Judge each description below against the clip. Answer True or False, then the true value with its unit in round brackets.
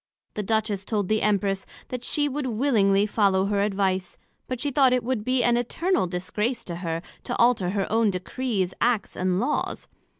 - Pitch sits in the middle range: False (215 Hz)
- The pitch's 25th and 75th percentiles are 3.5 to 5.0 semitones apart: True (4.2 semitones)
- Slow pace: False (180 wpm)